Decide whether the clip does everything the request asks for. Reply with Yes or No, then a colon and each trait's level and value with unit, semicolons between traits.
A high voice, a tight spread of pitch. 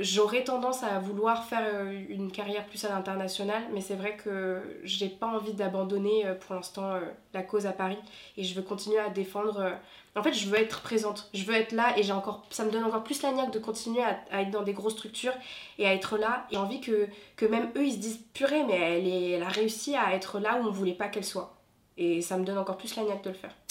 Yes: high, 205 Hz; narrow, 2.3 semitones